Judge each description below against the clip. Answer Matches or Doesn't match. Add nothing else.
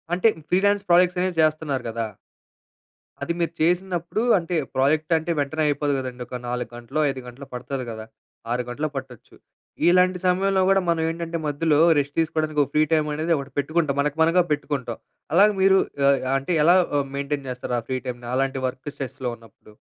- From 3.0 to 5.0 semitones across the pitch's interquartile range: Matches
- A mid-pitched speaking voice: Matches